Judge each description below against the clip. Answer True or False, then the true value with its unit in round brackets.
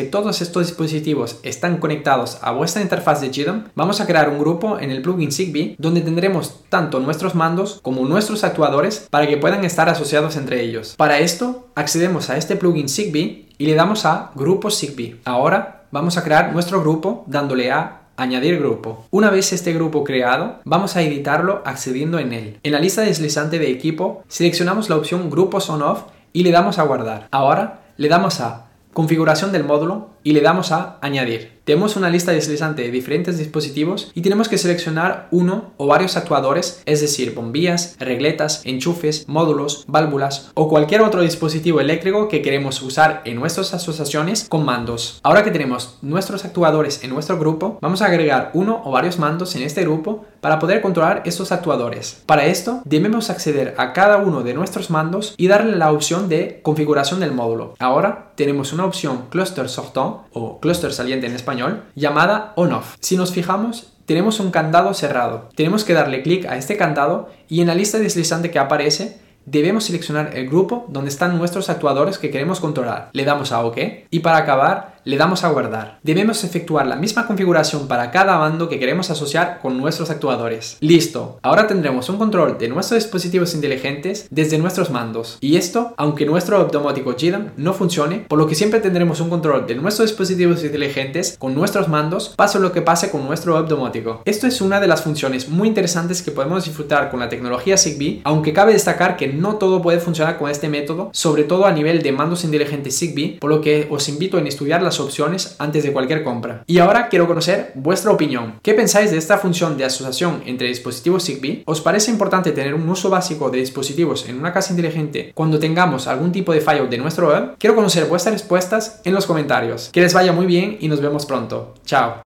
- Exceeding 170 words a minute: True (190 wpm)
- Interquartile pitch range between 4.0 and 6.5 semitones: True (4.3 semitones)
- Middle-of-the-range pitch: True (160 Hz)